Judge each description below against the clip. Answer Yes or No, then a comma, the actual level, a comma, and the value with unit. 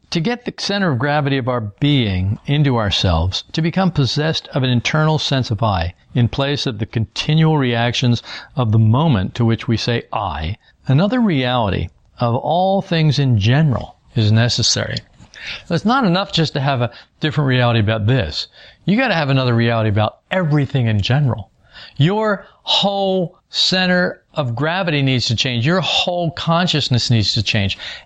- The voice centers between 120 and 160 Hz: Yes, low, 135 Hz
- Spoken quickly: No, average, 165 wpm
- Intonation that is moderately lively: No, wide, 6.1 semitones